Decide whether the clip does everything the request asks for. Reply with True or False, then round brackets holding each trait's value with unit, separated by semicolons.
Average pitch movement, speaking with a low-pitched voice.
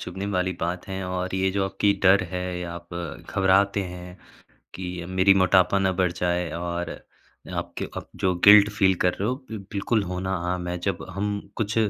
False (1.7 semitones; 95 Hz)